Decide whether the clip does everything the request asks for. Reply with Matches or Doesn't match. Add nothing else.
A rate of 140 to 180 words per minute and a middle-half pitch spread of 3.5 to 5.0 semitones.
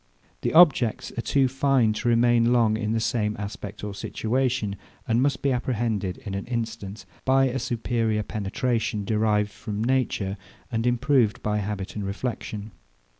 Doesn't match